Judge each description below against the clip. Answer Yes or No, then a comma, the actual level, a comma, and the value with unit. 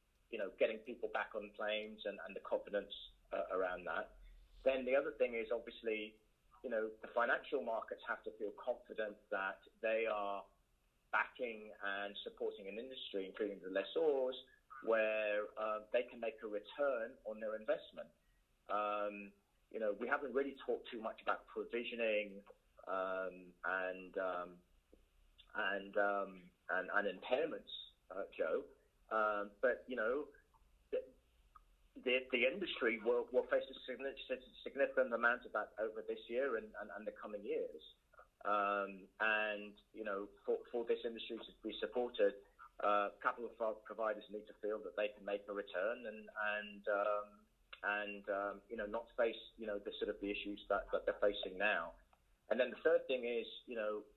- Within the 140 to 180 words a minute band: Yes, average, 165 wpm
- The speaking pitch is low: Yes, low, 105 Hz